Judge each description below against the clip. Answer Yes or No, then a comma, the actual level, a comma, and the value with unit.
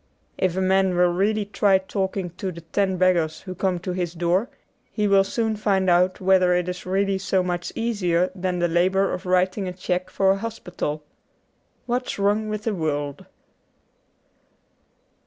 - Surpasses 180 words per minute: No, average, 175 wpm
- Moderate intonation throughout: No, narrow, 1.7 semitones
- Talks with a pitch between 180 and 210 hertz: Yes, medium, 185 Hz